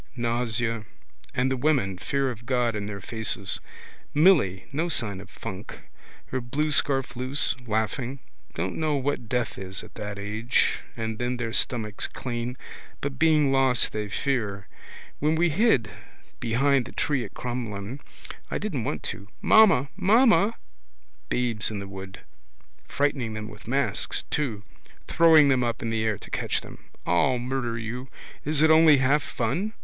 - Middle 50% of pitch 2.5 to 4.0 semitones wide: No, average, 4.5 semitones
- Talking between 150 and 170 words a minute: Yes, average, 155 wpm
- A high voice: No, low, 125 Hz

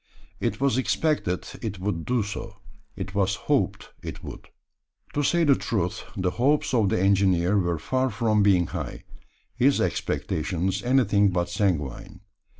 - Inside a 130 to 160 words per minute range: Yes, average, 150 wpm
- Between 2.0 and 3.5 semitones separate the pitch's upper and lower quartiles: No, average, 5.1 semitones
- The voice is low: Yes, low, 100 Hz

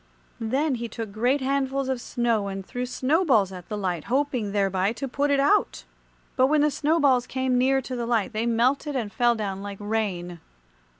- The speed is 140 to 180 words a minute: No, average, 190 wpm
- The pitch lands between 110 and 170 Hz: No, high, 240 Hz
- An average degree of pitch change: Yes, average, 4.6 semitones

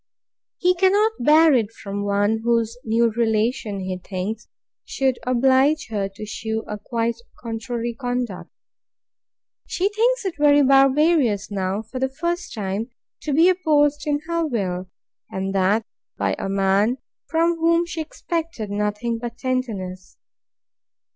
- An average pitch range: No, wide, 6.3 semitones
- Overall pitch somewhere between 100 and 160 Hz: No, high, 235 Hz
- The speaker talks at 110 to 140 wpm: Yes, slow, 135 wpm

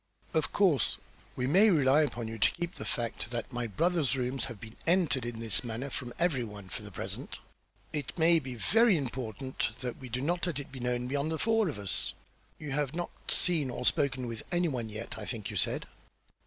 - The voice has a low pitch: Yes, low, 130 Hz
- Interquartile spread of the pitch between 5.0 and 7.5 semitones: Yes, average, 5.3 semitones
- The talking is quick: Yes, fast, 220 wpm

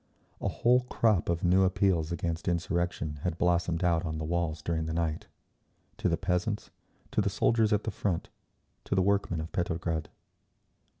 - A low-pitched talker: Yes, very low, 85 Hz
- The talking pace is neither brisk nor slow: Yes, average, 165 wpm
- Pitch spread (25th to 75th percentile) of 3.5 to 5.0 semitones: No, narrow, 2.4 semitones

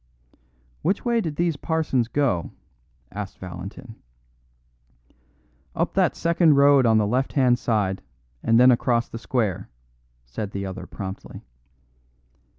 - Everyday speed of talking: No, slow, 125 wpm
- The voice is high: No, low, 120 Hz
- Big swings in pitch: Yes, wide, 6.2 semitones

